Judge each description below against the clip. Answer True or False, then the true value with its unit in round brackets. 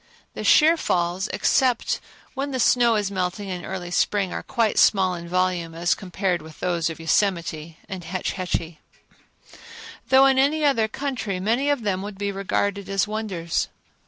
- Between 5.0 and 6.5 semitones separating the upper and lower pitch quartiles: False (4.3 semitones)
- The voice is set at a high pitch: True (195 Hz)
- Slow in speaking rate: False (165 wpm)